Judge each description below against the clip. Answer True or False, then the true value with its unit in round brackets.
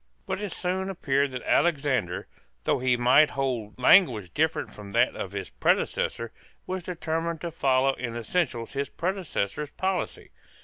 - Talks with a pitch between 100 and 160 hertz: True (140 Hz)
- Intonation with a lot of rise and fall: True (6.0 semitones)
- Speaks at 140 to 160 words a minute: True (145 wpm)